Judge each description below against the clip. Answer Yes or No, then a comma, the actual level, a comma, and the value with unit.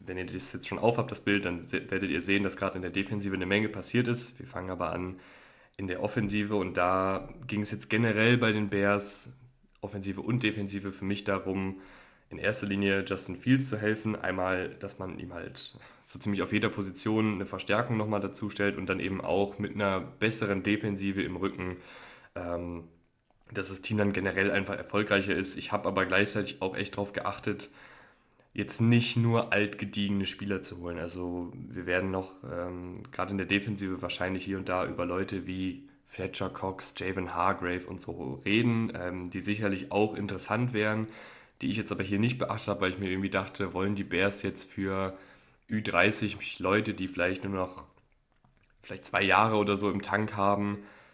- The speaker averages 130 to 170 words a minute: No, fast, 190 wpm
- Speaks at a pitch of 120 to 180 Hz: No, low, 100 Hz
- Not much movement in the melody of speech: Yes, narrow, 1.9 semitones